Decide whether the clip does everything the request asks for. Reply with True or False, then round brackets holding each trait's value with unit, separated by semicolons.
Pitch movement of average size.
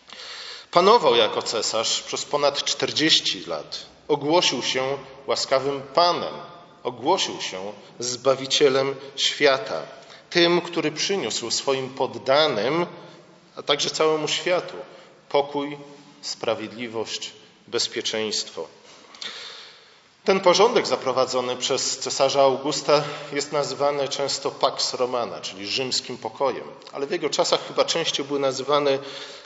True (3.3 semitones)